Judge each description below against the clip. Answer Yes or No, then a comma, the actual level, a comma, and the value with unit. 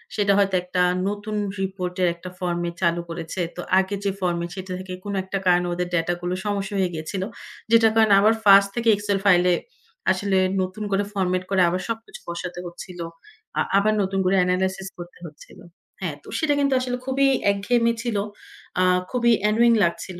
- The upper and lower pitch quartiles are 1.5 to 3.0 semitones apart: Yes, narrow, 2.5 semitones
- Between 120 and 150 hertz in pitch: No, high, 190 Hz